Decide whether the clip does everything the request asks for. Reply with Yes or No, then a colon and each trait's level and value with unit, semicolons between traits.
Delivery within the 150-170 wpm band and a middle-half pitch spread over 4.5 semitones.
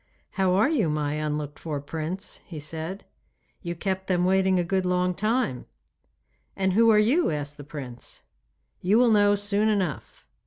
Yes: average, 165 wpm; average, 5.0 semitones